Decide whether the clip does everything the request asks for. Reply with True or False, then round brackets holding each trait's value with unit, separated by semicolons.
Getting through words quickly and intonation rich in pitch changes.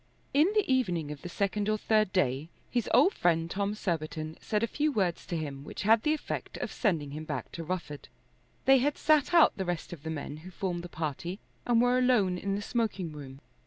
True (220 wpm; 6.4 semitones)